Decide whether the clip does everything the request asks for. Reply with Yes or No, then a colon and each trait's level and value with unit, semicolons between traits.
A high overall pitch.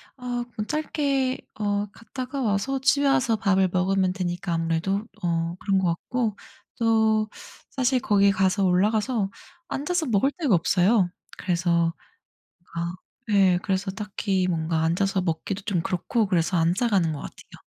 Yes: high, 200 Hz